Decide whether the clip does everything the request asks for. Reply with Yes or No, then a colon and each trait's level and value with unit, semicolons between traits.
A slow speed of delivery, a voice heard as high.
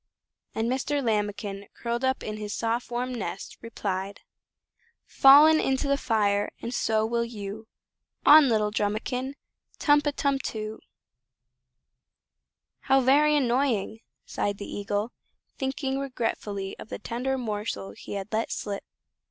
Yes: slow, 130 wpm; high, 230 Hz